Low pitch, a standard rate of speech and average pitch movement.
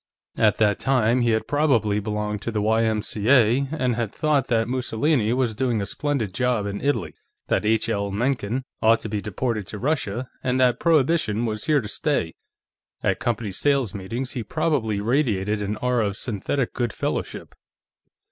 Yes: low, 115 Hz; average, 170 wpm; average, 3.7 semitones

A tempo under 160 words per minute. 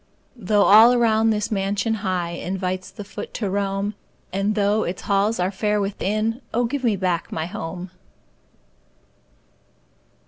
Yes: average, 140 wpm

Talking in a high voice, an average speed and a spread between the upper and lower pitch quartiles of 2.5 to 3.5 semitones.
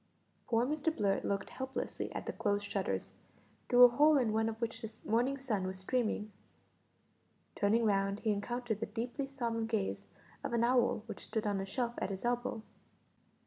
Yes: high, 230 Hz; average, 180 wpm; average, 3.0 semitones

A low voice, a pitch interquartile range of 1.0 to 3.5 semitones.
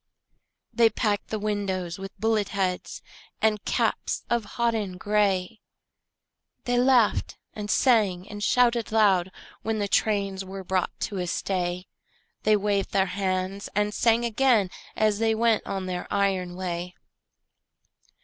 No: high, 205 Hz; average, 2.8 semitones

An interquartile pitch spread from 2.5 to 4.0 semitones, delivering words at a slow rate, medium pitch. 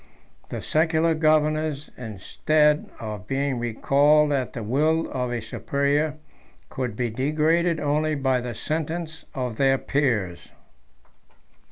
Yes: average, 3.6 semitones; slow, 120 wpm; medium, 145 Hz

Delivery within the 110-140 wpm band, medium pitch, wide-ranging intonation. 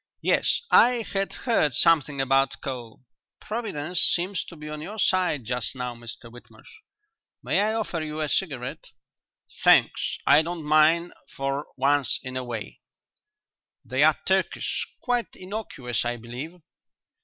Yes: slow, 135 wpm; medium, 150 Hz; wide, 6.1 semitones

